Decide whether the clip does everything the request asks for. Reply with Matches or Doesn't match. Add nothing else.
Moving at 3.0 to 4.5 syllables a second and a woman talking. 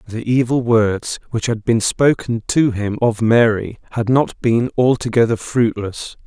Doesn't match